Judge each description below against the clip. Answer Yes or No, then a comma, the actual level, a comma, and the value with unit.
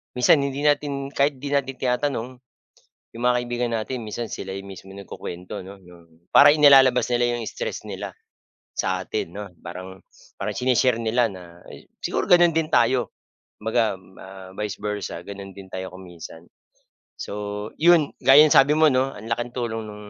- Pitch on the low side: Yes, low, 115 Hz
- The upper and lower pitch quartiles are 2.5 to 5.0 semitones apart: No, wide, 5.4 semitones